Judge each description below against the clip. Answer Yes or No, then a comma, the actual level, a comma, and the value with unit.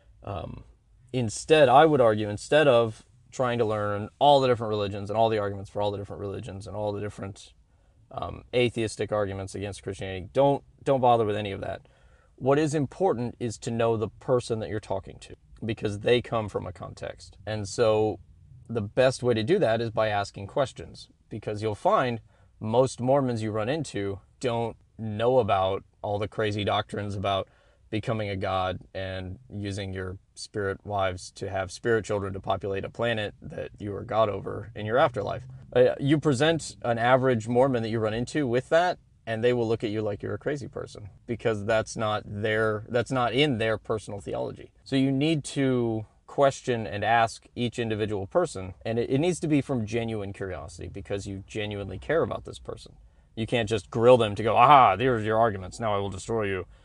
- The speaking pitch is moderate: No, low, 110 Hz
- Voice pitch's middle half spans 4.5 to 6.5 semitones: No, average, 3.2 semitones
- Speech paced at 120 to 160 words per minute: No, average, 195 wpm